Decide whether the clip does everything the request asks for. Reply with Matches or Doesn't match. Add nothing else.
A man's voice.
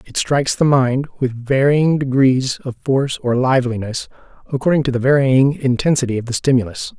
Matches